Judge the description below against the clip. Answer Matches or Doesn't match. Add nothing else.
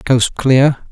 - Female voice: Doesn't match